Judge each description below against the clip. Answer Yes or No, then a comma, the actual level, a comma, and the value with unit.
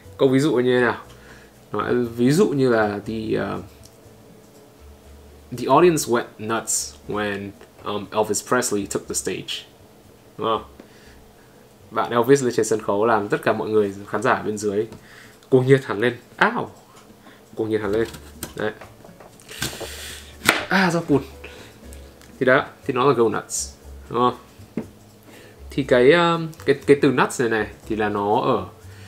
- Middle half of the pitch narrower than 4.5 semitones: Yes, average, 3.9 semitones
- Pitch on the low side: Yes, low, 110 Hz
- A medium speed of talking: No, slow, 160 wpm